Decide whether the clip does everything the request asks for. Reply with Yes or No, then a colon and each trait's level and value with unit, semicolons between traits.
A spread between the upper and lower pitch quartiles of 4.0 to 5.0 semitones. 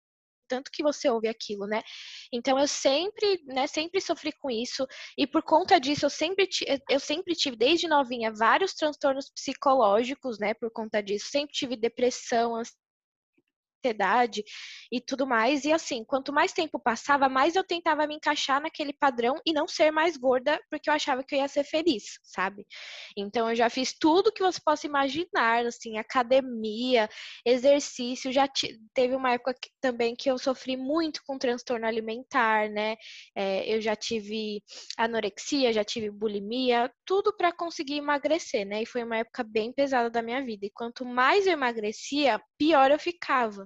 Yes: average, 4.5 semitones